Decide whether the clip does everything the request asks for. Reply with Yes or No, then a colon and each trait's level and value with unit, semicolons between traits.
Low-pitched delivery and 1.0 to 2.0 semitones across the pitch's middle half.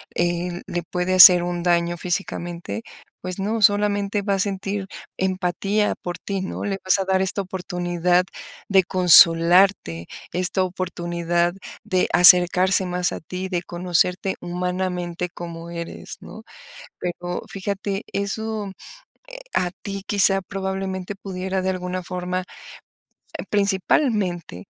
No: medium, 185 Hz; narrow, 1.7 semitones